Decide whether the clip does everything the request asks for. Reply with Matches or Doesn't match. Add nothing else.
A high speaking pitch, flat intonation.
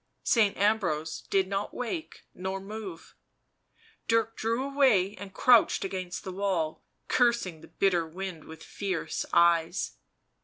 Doesn't match